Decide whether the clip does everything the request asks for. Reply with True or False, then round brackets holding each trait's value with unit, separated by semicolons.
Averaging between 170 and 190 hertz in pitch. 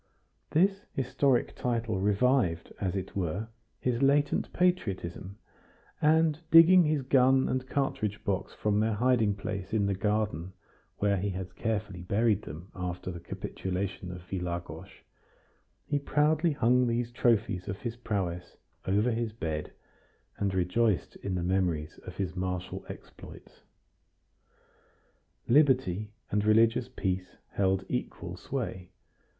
False (105 Hz)